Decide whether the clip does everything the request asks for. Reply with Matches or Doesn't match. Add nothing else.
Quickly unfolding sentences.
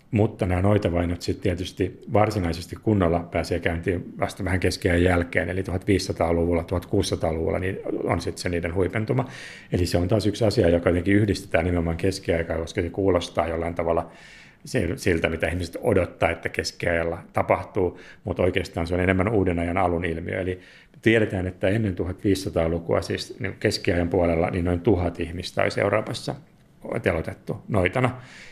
Doesn't match